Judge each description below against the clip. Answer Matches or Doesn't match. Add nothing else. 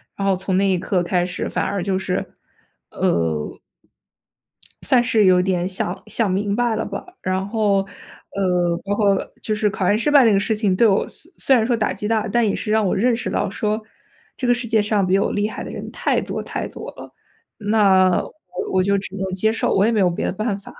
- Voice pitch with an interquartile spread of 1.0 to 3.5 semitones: Matches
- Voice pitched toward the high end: Matches